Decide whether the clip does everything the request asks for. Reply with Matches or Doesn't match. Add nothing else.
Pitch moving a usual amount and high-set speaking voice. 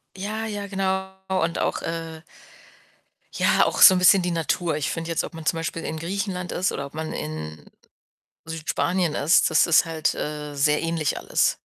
Doesn't match